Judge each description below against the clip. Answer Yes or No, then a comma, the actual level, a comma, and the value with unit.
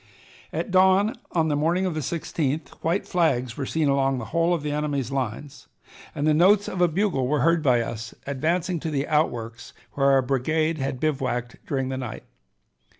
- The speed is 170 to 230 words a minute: Yes, average, 190 wpm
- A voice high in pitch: No, medium, 150 Hz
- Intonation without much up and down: No, average, 3.9 semitones